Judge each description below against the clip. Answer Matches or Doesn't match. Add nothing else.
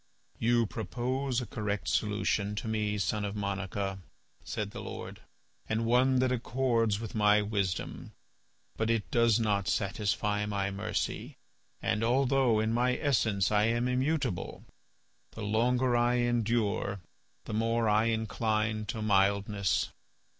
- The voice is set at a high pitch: Doesn't match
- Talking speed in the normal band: Doesn't match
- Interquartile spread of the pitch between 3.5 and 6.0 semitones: Doesn't match